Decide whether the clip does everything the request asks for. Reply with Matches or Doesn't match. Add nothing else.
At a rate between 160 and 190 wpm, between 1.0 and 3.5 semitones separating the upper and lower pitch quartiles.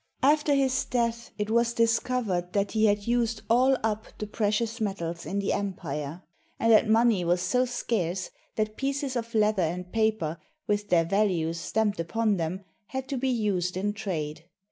Doesn't match